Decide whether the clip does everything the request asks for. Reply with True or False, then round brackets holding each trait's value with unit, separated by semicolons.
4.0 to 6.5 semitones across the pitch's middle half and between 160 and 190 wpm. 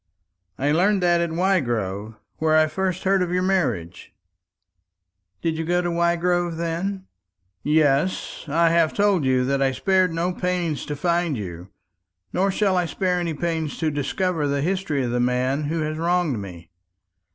True (4.3 semitones; 165 wpm)